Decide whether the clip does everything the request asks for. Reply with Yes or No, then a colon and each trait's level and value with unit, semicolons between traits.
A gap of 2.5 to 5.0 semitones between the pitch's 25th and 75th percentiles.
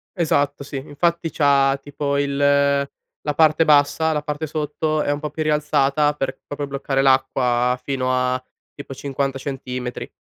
No: narrow, 1.7 semitones